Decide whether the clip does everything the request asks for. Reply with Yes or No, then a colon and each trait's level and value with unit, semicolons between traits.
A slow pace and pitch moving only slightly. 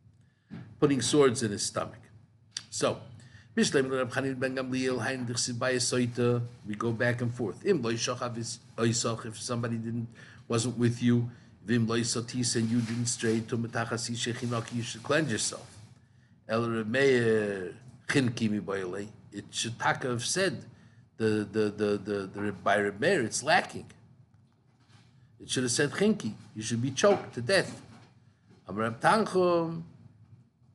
Yes: slow, 100 wpm; narrow, 1.8 semitones